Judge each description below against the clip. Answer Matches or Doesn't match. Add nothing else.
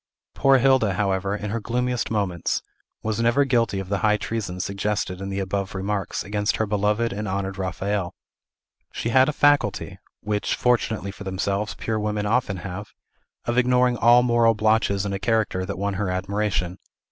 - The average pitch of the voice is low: Matches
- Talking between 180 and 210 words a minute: Doesn't match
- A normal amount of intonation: Matches